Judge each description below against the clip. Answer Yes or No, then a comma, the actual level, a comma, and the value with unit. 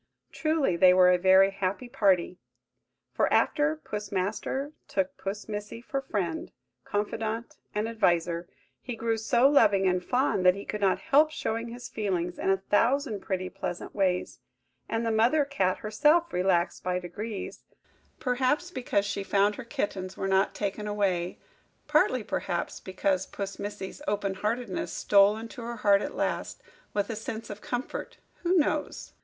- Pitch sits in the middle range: No, high, 205 Hz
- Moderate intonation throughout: Yes, average, 3.8 semitones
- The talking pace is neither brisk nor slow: Yes, average, 155 wpm